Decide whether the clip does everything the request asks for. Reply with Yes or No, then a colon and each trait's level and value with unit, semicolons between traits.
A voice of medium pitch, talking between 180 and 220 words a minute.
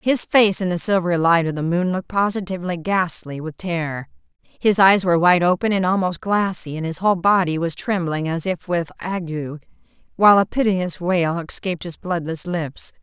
Yes: medium, 175 Hz; average, 185 wpm